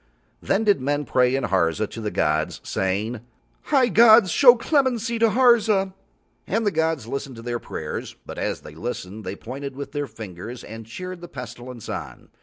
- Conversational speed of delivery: Yes, average, 180 wpm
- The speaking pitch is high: No, low, 135 Hz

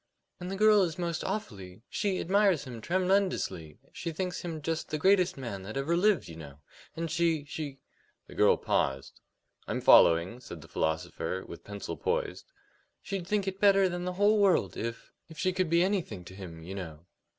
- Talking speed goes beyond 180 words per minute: Yes, average, 190 wpm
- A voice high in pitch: No, medium, 165 Hz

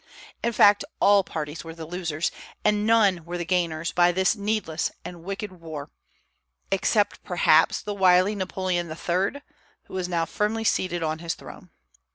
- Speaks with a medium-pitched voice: Yes, medium, 180 Hz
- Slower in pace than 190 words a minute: Yes, average, 160 wpm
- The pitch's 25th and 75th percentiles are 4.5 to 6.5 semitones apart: No, average, 3.4 semitones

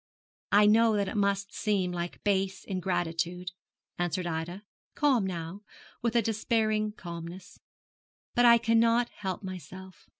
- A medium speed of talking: No, slow, 130 wpm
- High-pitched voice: Yes, high, 195 Hz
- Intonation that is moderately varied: Yes, average, 3.5 semitones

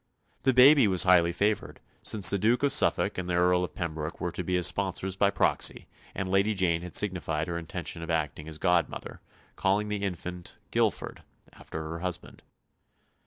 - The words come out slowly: No, average, 180 wpm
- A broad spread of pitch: No, average, 2.8 semitones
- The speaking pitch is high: No, very low, 90 Hz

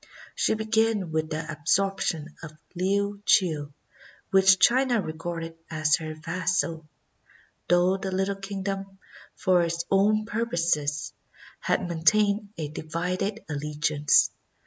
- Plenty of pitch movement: No, average, 3.9 semitones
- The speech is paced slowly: Yes, slow, 105 wpm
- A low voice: No, medium, 180 Hz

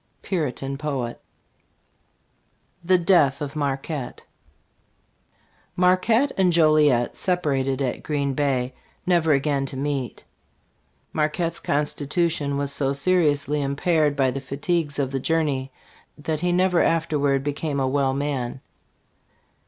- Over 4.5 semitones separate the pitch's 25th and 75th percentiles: No, average, 3.1 semitones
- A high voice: No, medium, 145 Hz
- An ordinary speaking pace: No, slow, 115 wpm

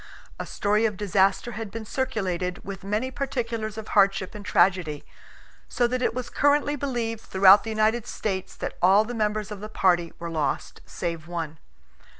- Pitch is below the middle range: No, high, 210 Hz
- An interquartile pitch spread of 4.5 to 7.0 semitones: No, average, 3.4 semitones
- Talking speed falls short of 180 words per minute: Yes, average, 170 wpm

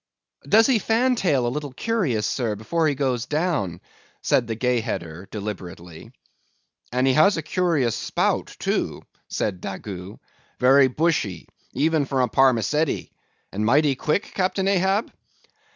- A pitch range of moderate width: No, wide, 7.3 semitones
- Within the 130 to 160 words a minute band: Yes, average, 140 wpm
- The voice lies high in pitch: No, low, 135 Hz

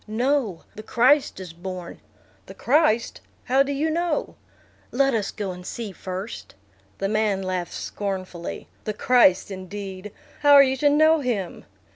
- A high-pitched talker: Yes, high, 215 Hz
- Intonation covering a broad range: Yes, wide, 6.5 semitones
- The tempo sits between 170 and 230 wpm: No, average, 150 wpm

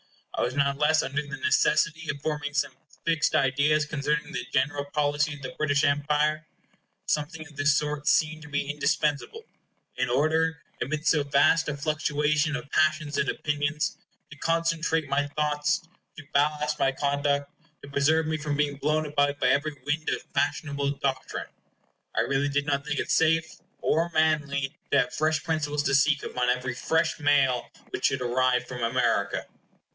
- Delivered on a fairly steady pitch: Yes, narrow, 1.6 semitones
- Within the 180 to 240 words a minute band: No, average, 170 wpm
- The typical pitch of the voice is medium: Yes, medium, 145 Hz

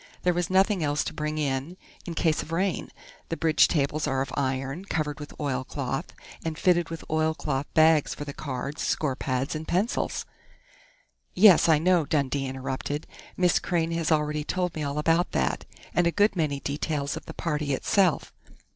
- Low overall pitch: No, medium, 155 Hz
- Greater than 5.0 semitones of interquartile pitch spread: No, average, 3.2 semitones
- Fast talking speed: No, average, 180 wpm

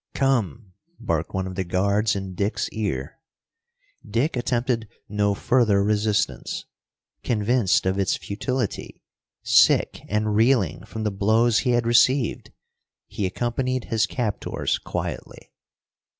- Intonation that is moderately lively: Yes, average, 3.3 semitones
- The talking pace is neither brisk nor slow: No, slow, 120 wpm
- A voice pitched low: Yes, low, 105 Hz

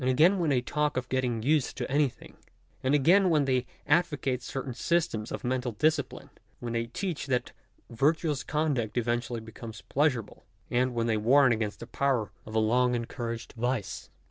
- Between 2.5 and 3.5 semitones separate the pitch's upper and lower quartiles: No, average, 3.9 semitones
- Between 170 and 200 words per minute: Yes, average, 180 wpm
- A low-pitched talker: Yes, low, 125 Hz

